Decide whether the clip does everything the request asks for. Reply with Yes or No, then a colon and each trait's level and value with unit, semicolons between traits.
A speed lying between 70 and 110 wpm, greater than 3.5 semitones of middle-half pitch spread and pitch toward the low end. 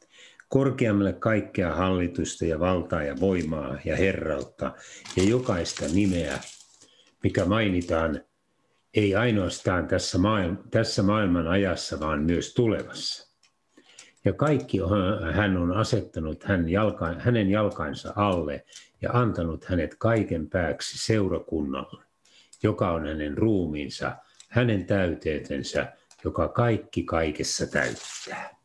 Yes: average, 105 wpm; average, 3.9 semitones; very low, 95 Hz